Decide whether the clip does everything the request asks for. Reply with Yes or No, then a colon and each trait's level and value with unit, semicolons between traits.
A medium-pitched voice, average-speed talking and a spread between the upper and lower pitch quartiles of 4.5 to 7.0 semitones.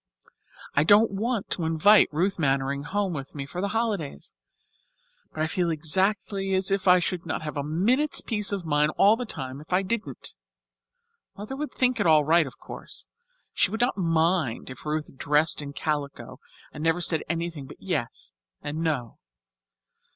Yes: medium, 165 Hz; average, 175 wpm; average, 5.0 semitones